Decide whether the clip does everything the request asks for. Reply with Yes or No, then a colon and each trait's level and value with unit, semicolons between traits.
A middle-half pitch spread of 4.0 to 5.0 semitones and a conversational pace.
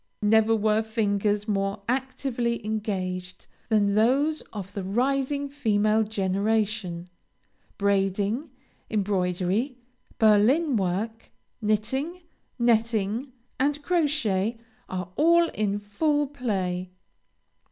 No: average, 4.4 semitones; slow, 90 wpm